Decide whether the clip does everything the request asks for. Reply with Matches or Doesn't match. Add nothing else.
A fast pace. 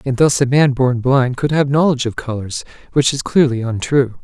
Matches